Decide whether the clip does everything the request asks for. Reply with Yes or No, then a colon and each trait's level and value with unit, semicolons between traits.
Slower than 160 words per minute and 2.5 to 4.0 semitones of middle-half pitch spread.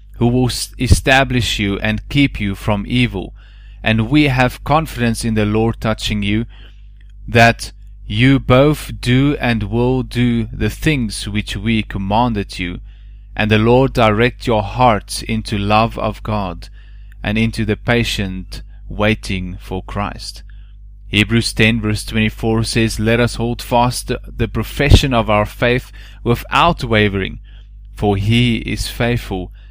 Yes: slow, 135 wpm; average, 2.8 semitones